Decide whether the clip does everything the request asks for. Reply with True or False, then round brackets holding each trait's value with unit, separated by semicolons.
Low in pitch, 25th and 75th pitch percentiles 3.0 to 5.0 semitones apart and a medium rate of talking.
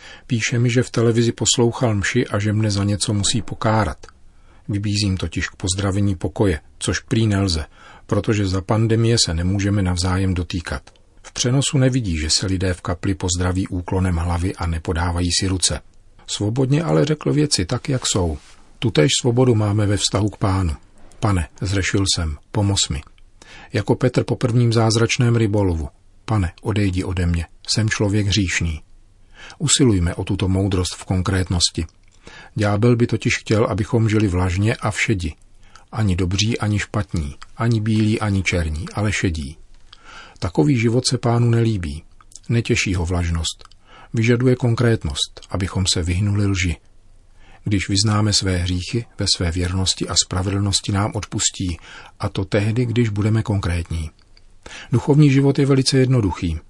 True (100 Hz; 3.7 semitones; 145 wpm)